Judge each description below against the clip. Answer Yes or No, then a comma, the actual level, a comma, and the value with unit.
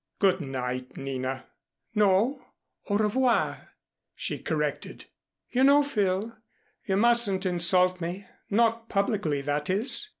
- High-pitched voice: Yes, high, 195 Hz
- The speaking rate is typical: No, slow, 110 wpm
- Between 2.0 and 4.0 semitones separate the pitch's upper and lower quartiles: No, wide, 5.6 semitones